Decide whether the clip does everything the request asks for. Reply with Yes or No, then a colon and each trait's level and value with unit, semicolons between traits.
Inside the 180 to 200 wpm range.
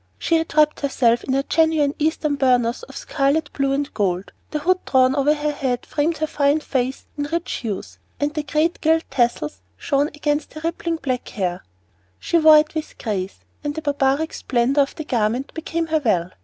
Yes: average, 195 wpm